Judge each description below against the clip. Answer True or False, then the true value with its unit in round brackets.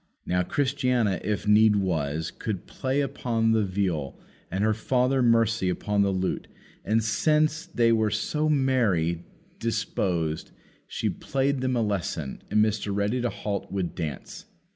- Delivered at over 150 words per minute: False (145 wpm)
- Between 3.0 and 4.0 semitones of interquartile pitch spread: False (4.9 semitones)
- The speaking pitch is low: True (110 Hz)